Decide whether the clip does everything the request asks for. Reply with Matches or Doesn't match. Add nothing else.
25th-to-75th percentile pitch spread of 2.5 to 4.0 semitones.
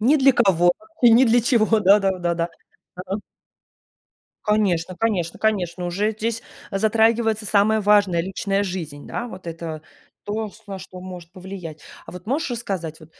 Matches